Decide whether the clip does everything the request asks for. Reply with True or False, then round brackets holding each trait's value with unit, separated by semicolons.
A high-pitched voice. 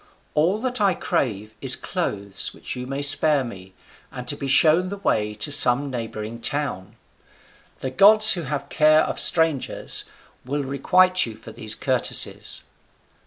False (140 Hz)